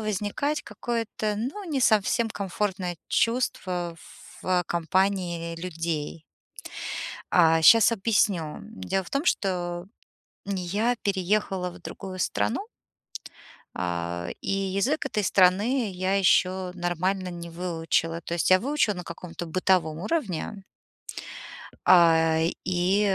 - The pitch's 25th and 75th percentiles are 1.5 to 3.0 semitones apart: No, average, 3.4 semitones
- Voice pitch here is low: No, medium, 185 Hz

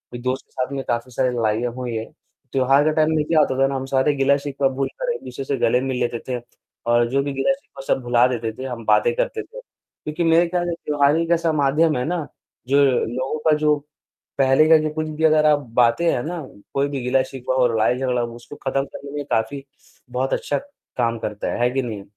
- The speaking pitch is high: No, low, 135 Hz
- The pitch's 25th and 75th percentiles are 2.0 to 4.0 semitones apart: Yes, average, 3.5 semitones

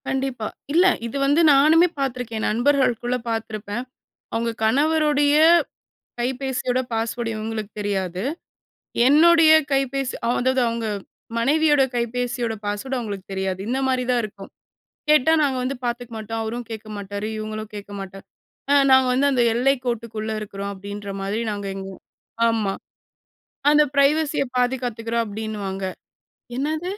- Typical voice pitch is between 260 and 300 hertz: No, high, 235 Hz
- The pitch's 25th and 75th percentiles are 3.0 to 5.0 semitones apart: Yes, average, 4.0 semitones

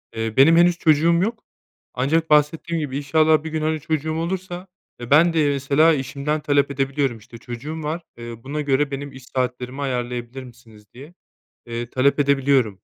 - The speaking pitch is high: No, medium, 140 Hz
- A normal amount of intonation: Yes, average, 3.6 semitones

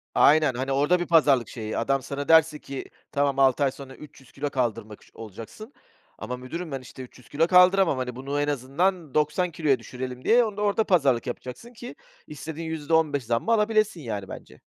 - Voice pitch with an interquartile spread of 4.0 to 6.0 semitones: Yes, average, 4.6 semitones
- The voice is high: No, medium, 145 Hz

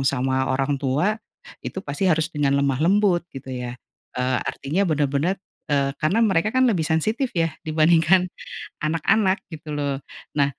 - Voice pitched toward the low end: No, medium, 155 Hz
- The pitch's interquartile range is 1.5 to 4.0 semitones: No, average, 5.0 semitones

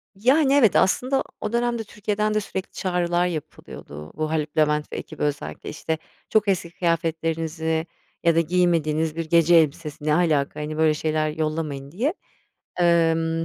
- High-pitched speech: No, medium, 165 Hz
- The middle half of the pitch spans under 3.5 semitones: Yes, average, 2.8 semitones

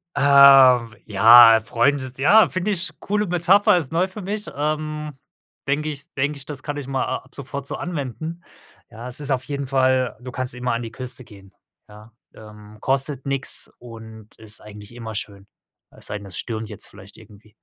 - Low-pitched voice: Yes, low, 130 Hz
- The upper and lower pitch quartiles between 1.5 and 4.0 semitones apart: No, average, 4.7 semitones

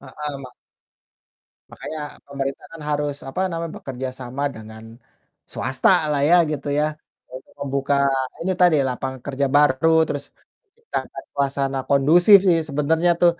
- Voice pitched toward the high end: No, medium, 140 Hz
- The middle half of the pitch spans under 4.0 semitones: Yes, average, 3.3 semitones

